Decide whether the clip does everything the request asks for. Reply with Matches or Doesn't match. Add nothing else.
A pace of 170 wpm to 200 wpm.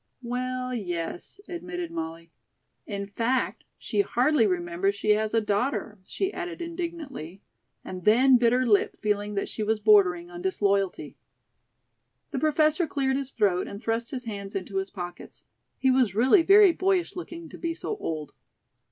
Doesn't match